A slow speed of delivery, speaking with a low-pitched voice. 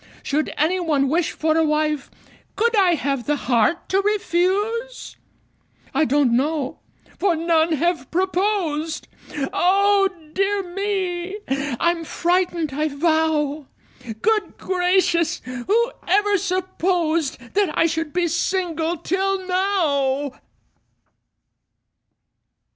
No: slow, 105 wpm; very high, 340 Hz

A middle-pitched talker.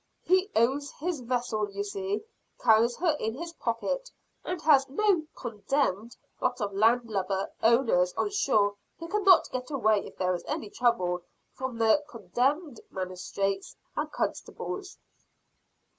No: high, 235 Hz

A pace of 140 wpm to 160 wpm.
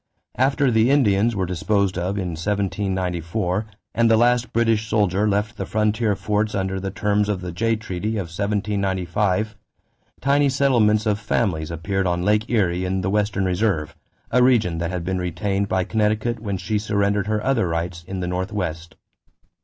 No: average, 170 wpm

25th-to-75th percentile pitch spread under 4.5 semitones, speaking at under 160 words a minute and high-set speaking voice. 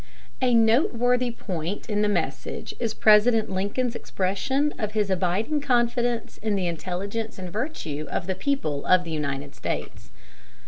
No: average, 4.9 semitones; average, 145 wpm; high, 210 Hz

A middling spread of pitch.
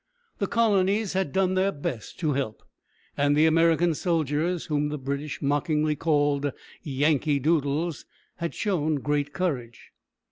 Yes: average, 3.3 semitones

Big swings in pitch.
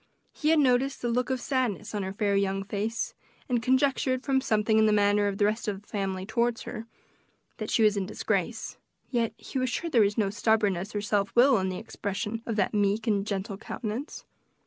No: average, 3.2 semitones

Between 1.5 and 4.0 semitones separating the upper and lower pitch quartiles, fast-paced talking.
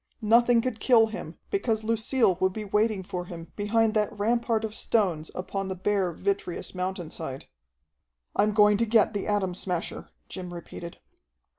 No: average, 3.4 semitones; average, 155 wpm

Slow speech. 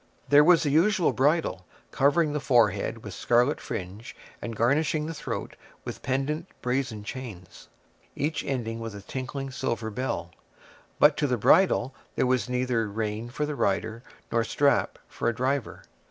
No: average, 155 wpm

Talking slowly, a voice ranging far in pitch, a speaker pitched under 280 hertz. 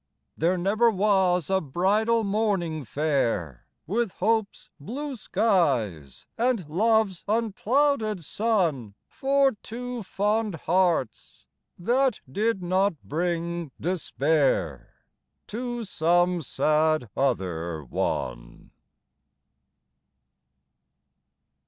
Yes: slow, 80 wpm; wide, 6.5 semitones; medium, 185 Hz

